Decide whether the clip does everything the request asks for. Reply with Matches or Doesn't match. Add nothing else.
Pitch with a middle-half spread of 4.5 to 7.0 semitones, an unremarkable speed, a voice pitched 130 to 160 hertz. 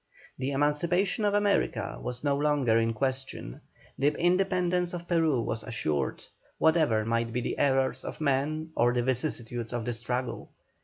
Matches